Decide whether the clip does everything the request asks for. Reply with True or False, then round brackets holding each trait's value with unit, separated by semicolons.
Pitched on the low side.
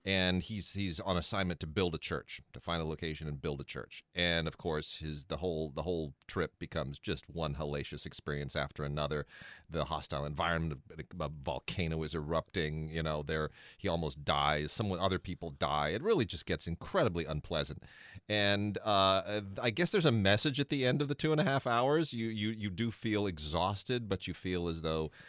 True (85 Hz)